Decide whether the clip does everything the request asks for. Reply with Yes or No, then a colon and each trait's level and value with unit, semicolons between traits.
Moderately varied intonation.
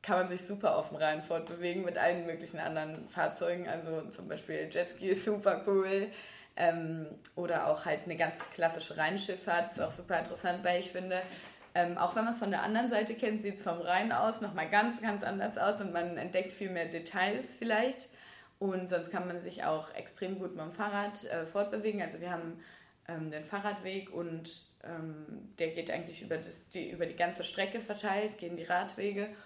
Yes: average, 3.4 semitones